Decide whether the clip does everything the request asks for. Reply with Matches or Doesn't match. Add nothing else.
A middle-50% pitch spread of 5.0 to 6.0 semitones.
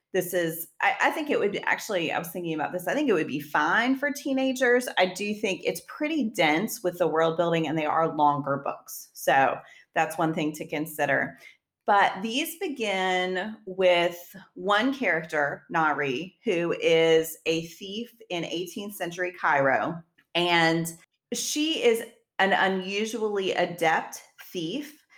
Matches